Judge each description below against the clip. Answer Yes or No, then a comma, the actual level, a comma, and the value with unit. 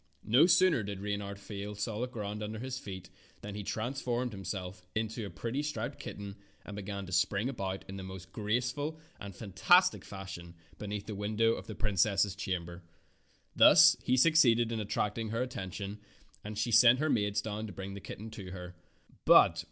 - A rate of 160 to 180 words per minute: Yes, average, 175 wpm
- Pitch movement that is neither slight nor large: Yes, average, 3.0 semitones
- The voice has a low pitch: Yes, low, 105 Hz